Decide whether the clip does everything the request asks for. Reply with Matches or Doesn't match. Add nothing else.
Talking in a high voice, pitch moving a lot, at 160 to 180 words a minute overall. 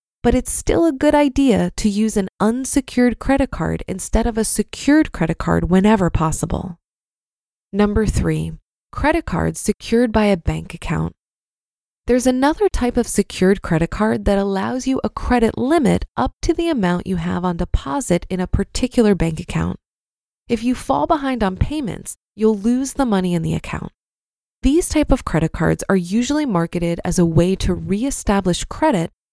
Matches